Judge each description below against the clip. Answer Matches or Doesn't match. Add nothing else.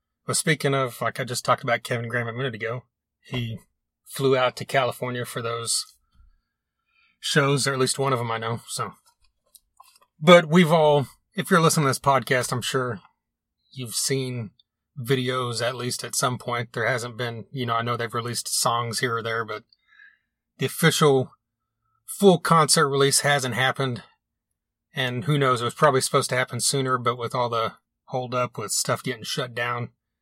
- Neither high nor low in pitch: Doesn't match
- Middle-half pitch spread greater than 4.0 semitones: Doesn't match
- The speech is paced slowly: Doesn't match